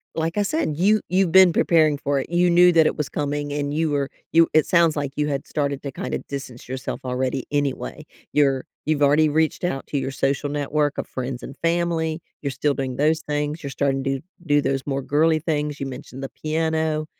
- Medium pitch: Yes, medium, 150 Hz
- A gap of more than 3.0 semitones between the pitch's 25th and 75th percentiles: No, narrow, 2.6 semitones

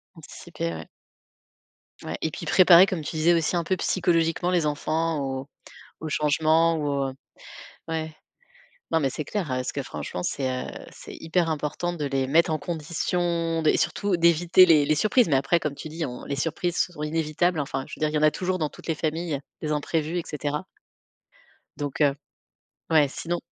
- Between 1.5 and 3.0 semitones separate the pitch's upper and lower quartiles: Yes, narrow, 2.5 semitones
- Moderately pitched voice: Yes, medium, 160 Hz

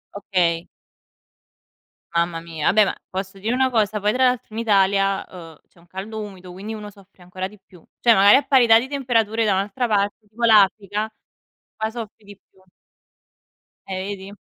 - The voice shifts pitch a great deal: No, average, 2.7 semitones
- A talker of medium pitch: No, high, 205 Hz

